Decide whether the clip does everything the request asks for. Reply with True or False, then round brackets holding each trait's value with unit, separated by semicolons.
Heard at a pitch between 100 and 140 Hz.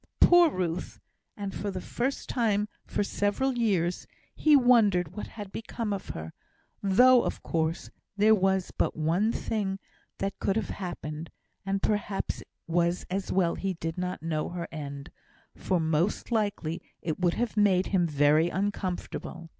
False (190 Hz)